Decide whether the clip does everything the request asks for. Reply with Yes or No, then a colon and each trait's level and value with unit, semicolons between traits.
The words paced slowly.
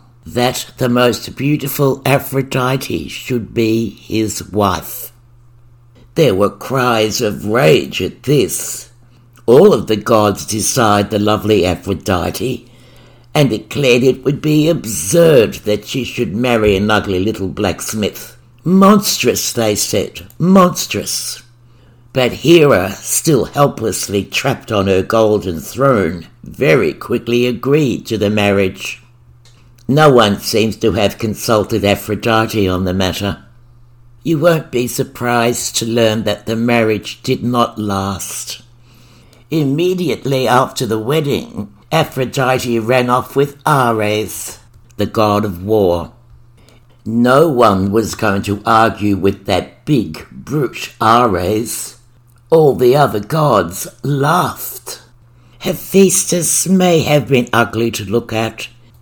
Yes: slow, 120 wpm